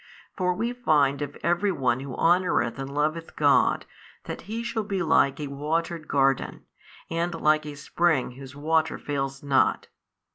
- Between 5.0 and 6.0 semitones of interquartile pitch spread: No, average, 3.8 semitones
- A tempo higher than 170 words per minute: No, average, 155 wpm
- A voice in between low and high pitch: Yes, medium, 155 Hz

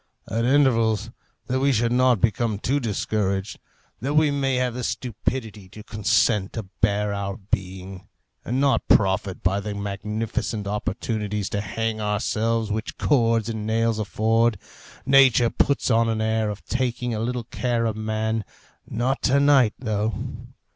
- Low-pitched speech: Yes, low, 110 Hz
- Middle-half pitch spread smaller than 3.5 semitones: Yes, average, 2.7 semitones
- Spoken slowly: No, average, 150 wpm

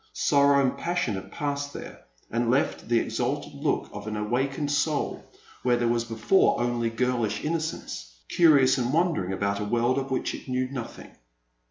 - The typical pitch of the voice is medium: No, low, 125 Hz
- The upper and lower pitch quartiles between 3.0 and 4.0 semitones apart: Yes, average, 3.7 semitones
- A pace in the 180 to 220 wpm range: No, average, 170 wpm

